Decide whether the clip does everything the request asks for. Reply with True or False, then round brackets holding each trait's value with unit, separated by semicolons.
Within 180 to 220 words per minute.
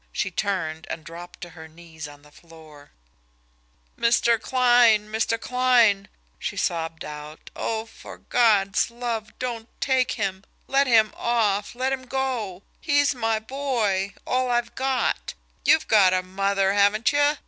False (145 wpm)